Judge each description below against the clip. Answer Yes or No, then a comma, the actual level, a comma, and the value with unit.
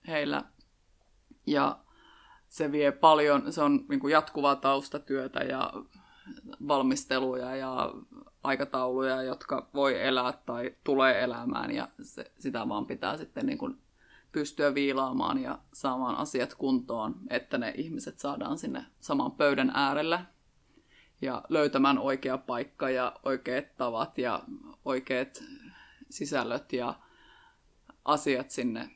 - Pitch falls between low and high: Yes, medium, 145 Hz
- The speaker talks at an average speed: Yes, average, 115 wpm